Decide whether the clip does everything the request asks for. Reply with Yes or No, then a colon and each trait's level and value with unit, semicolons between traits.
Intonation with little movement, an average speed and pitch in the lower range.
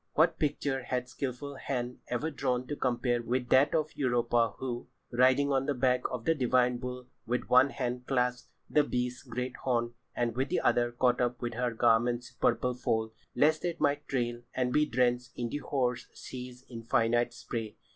Yes: narrow, 1.6 semitones; average, 175 wpm; low, 125 Hz